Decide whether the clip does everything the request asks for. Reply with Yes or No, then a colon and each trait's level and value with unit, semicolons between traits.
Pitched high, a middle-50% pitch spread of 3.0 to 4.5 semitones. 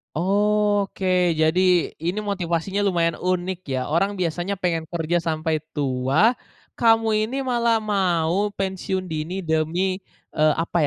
No: medium, 180 Hz; average, 3.6 semitones